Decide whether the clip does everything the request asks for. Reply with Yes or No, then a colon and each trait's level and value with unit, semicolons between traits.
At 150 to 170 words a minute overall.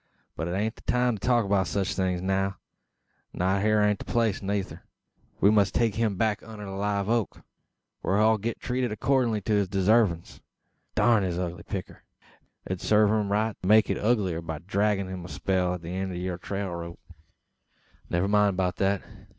No: average, 190 wpm